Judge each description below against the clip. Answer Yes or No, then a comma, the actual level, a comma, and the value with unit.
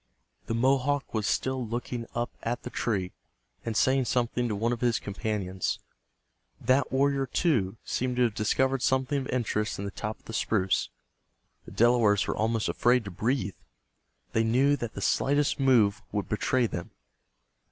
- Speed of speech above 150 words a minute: Yes, average, 165 wpm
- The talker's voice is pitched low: Yes, low, 120 Hz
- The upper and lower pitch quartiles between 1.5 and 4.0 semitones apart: Yes, average, 3.5 semitones